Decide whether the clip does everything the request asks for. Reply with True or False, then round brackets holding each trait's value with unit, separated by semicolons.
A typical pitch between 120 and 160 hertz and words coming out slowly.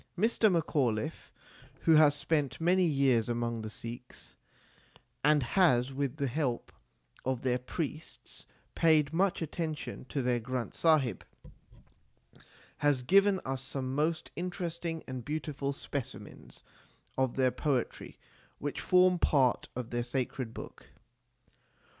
True (140 Hz; 120 wpm)